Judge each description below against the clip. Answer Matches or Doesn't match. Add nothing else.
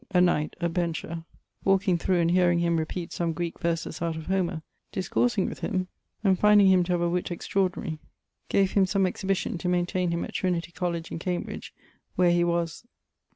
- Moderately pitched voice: Matches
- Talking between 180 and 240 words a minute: Matches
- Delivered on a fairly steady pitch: Matches